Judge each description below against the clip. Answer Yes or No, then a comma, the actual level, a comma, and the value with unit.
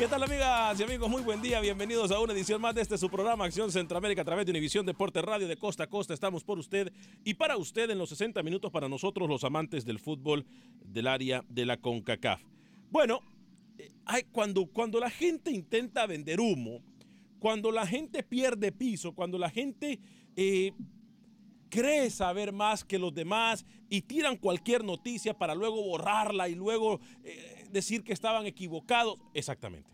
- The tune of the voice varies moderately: Yes, average, 4.2 semitones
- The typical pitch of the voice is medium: No, high, 210 Hz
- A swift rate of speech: No, average, 180 wpm